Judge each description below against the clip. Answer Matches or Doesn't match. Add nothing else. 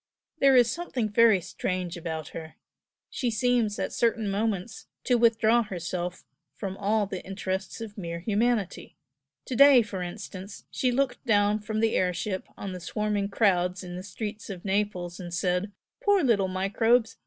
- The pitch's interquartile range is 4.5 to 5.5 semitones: Doesn't match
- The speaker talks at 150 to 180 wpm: Matches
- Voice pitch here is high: Matches